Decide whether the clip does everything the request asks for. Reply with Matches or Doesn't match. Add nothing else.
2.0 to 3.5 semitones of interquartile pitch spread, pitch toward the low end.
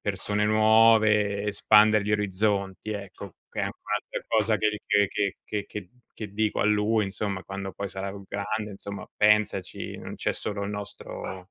Doesn't match